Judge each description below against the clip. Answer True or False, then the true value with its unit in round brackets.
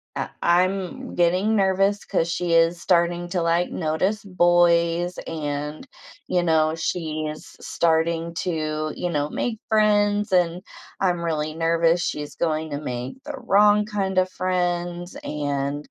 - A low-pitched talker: False (175 Hz)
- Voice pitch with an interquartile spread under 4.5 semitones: True (2.8 semitones)